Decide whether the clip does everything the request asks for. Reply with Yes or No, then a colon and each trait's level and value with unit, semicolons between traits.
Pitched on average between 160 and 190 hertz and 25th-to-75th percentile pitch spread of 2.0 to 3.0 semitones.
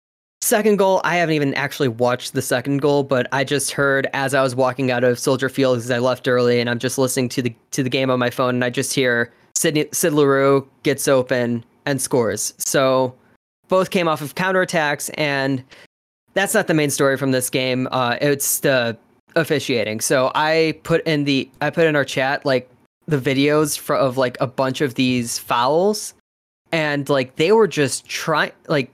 No: low, 135 Hz; average, 2.7 semitones